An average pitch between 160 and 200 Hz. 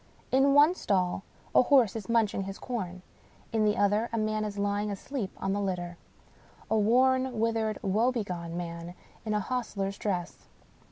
No: high, 210 Hz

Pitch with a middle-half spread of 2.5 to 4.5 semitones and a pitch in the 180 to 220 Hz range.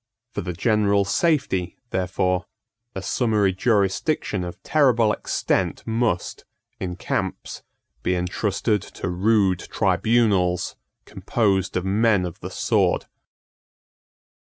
No: average, 3.5 semitones; low, 100 Hz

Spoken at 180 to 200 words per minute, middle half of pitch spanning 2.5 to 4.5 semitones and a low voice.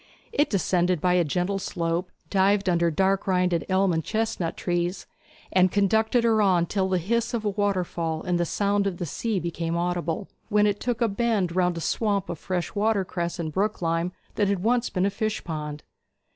No: average, 190 wpm; average, 2.9 semitones; medium, 185 Hz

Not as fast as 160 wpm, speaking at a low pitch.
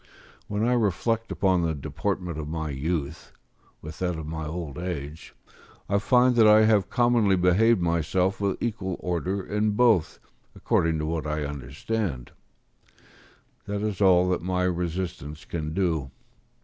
Yes: average, 150 wpm; very low, 90 Hz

